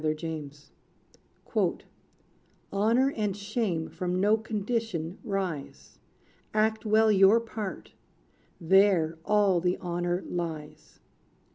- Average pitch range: Yes, average, 4.3 semitones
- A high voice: Yes, high, 195 Hz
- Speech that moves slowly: Yes, slow, 95 wpm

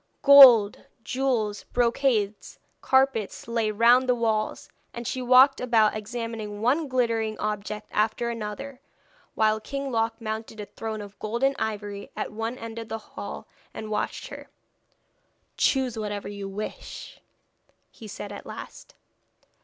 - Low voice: No, high, 225 Hz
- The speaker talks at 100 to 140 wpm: Yes, slow, 135 wpm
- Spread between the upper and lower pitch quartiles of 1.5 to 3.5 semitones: Yes, narrow, 2.6 semitones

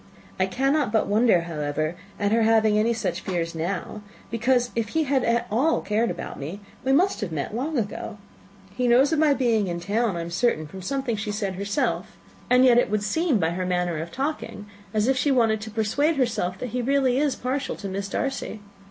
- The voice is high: Yes, high, 220 Hz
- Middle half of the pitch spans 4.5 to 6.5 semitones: Yes, average, 5.0 semitones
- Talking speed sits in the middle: No, fast, 215 wpm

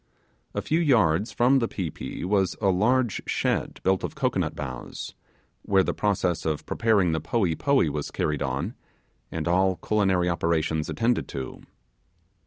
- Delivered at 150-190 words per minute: Yes, average, 155 wpm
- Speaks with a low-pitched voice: Yes, very low, 95 Hz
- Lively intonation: Yes, wide, 5.7 semitones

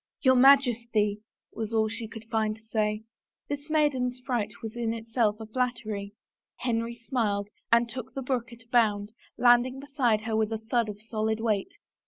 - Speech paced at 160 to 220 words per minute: Yes, average, 190 wpm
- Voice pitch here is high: Yes, high, 230 Hz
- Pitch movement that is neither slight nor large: No, narrow, 2.3 semitones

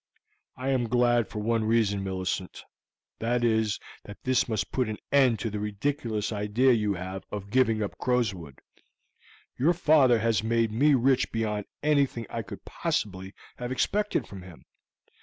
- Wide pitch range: No, average, 3.4 semitones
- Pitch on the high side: No, low, 115 Hz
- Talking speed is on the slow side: No, average, 160 wpm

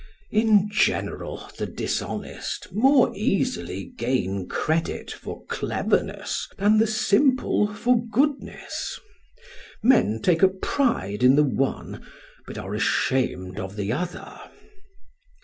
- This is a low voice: No, high, 200 Hz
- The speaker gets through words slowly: Yes, slow, 110 wpm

